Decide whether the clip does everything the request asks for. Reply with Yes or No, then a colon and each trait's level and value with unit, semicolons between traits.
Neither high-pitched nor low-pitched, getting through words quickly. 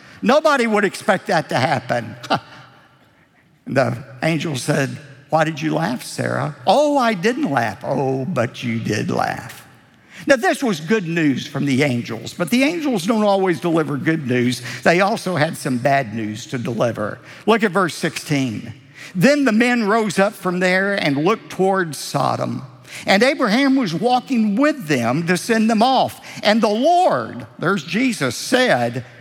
No: medium, 180 Hz; average, 160 wpm